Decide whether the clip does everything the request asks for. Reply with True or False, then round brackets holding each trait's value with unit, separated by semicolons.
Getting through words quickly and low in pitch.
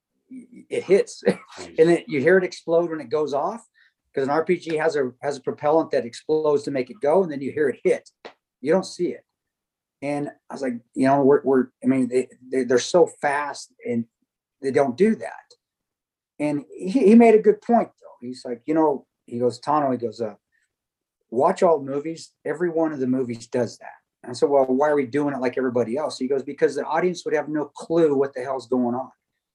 False (225 wpm; 150 Hz)